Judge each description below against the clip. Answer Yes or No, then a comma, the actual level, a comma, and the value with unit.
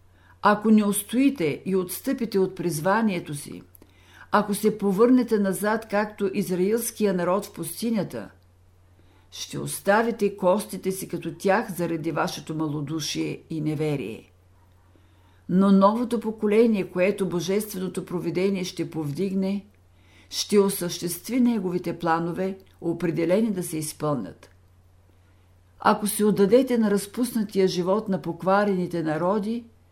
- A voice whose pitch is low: No, medium, 185 Hz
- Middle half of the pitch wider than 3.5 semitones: Yes, average, 5.1 semitones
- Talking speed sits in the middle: No, slow, 105 wpm